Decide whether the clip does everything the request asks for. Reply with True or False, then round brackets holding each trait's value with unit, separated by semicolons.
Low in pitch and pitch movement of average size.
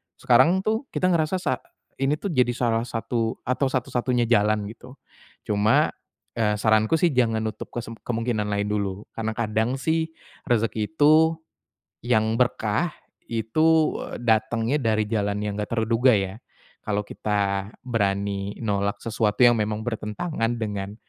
True (115 Hz; 3.1 semitones)